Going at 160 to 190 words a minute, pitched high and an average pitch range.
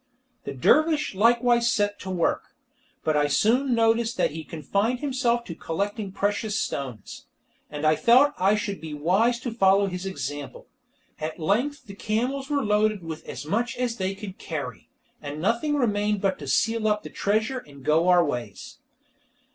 No: average, 170 wpm; high, 205 Hz; wide, 6.5 semitones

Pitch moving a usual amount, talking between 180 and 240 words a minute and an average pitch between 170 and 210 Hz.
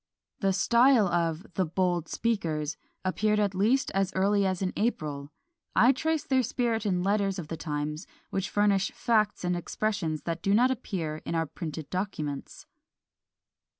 No: average, 4.4 semitones; average, 155 wpm; high, 190 Hz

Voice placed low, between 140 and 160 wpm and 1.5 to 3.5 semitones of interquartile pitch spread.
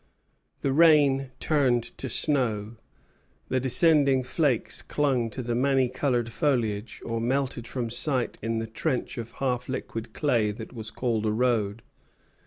Yes: low, 125 Hz; average, 145 wpm; average, 3.0 semitones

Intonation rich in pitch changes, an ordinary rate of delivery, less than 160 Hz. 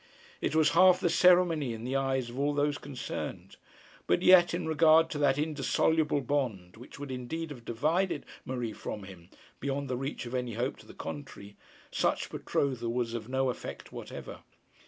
No: average, 4.3 semitones; average, 180 wpm; low, 135 Hz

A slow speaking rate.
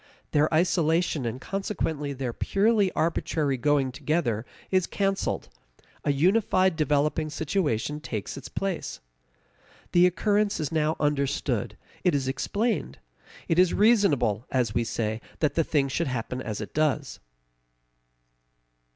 Yes: slow, 125 wpm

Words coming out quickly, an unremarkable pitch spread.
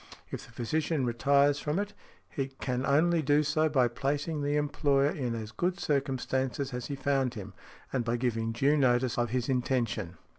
No: average, 180 wpm; average, 3.1 semitones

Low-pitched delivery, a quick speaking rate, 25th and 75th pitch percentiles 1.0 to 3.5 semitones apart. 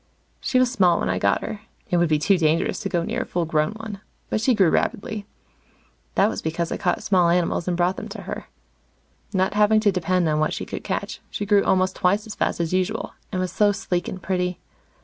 No: medium, 185 Hz; fast, 230 wpm; average, 3.2 semitones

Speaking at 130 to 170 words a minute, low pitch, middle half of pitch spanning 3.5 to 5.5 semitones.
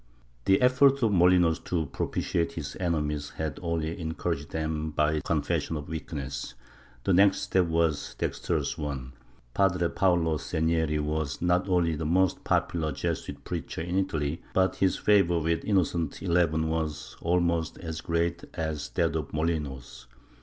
No: average, 155 wpm; very low, 80 Hz; narrow, 2.4 semitones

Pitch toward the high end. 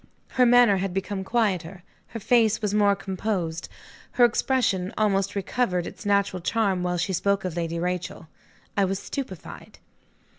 Yes: high, 195 Hz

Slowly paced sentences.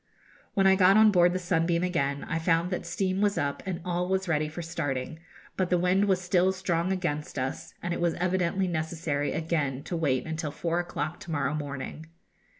No: average, 200 wpm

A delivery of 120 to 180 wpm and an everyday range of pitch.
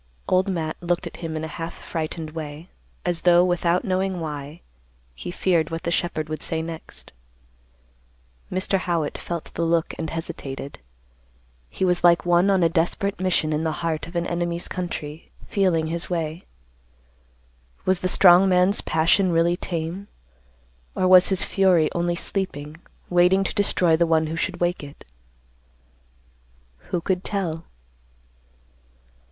No: average, 150 wpm; narrow, 2.1 semitones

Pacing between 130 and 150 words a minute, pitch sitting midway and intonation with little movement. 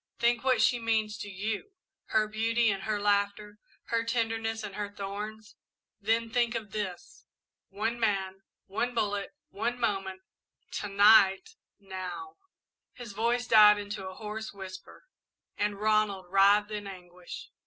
No: average, 140 wpm; high, 210 Hz; narrow, 2.2 semitones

